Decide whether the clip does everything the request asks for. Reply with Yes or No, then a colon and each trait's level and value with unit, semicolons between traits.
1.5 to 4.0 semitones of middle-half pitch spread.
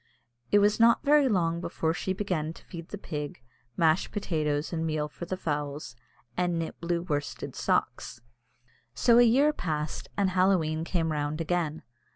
Yes: average, 3.7 semitones